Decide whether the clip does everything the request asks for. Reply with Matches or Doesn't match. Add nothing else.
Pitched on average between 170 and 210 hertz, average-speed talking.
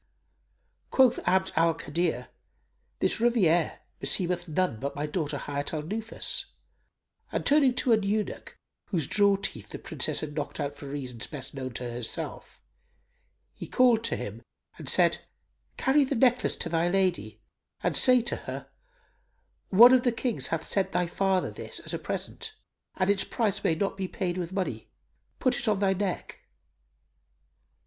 Matches